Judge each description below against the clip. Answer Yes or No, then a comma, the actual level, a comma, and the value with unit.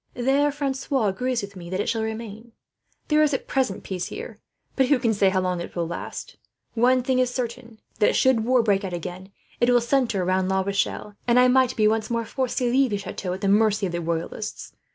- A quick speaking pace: Yes, fast, 230 wpm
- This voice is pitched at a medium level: No, high, 225 Hz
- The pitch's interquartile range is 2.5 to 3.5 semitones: No, average, 4.7 semitones